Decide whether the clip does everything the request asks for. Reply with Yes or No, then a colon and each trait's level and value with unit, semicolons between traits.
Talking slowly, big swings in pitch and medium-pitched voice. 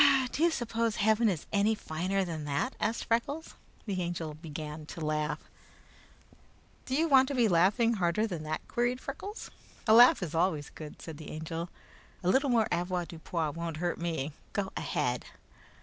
No: average, 165 wpm; wide, 6.3 semitones; medium, 180 Hz